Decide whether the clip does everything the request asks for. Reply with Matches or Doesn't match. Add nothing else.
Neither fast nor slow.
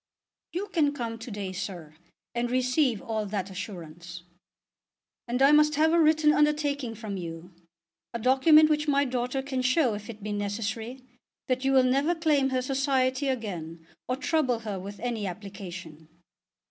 Matches